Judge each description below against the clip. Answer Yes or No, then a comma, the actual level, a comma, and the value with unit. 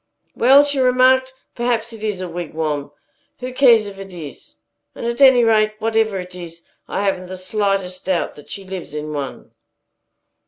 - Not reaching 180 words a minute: Yes, average, 170 wpm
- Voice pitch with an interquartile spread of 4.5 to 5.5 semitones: Yes, average, 4.8 semitones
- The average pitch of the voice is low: No, high, 200 Hz